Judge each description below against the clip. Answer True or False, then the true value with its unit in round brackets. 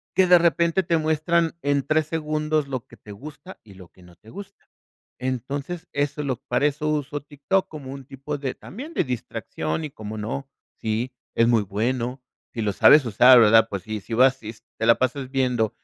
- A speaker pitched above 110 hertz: True (135 Hz)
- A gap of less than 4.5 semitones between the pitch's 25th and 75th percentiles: False (4.9 semitones)